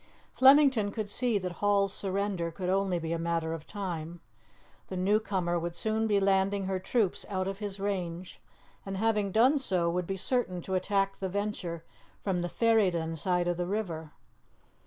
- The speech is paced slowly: No, average, 180 wpm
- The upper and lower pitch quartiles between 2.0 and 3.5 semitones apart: Yes, average, 2.8 semitones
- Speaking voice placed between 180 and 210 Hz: Yes, high, 190 Hz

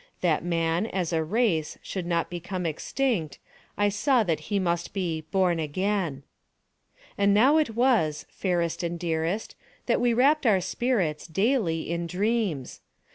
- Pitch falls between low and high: Yes, medium, 180 Hz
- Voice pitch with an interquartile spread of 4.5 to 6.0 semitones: Yes, average, 4.8 semitones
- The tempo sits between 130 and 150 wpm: Yes, average, 145 wpm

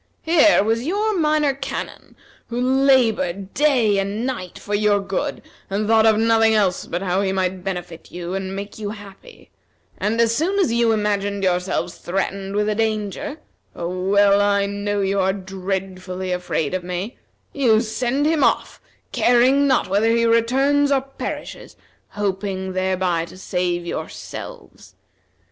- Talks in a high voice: Yes, high, 205 Hz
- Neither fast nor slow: Yes, average, 155 wpm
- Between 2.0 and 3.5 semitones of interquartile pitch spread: No, average, 4.0 semitones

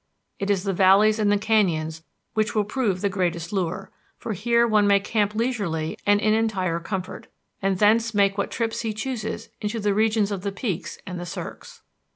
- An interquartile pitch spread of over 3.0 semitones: No, narrow, 2.5 semitones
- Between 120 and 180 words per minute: No, average, 190 wpm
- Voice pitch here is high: Yes, high, 205 Hz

